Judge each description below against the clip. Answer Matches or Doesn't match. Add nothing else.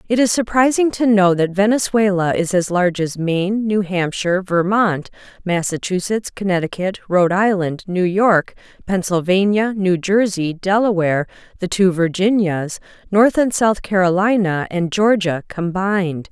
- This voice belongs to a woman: Matches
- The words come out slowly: Matches